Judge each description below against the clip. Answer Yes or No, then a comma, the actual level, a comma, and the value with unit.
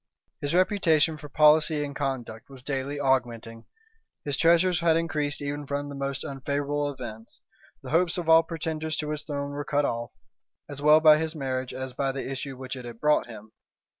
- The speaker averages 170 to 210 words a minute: Yes, average, 190 wpm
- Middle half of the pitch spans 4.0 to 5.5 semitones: No, average, 2.7 semitones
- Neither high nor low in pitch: Yes, medium, 145 Hz